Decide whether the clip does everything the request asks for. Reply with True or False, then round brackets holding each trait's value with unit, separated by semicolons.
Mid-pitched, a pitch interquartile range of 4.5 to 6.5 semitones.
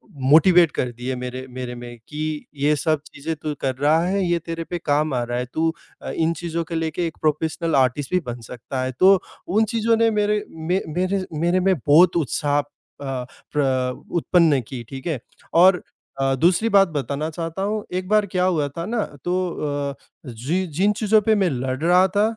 True (160 Hz; 5.2 semitones)